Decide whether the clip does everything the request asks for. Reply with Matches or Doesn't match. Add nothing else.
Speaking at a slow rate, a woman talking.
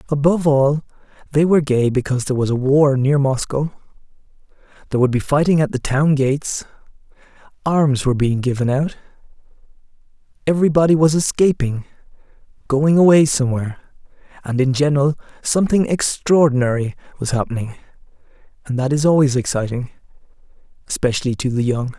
Doesn't match